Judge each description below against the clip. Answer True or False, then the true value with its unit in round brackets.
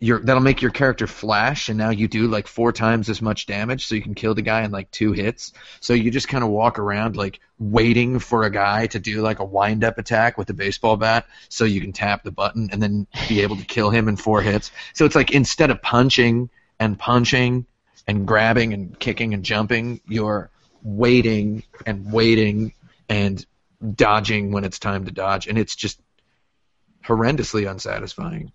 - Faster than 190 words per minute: True (200 wpm)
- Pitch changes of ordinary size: False (2.2 semitones)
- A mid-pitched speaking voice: False (110 Hz)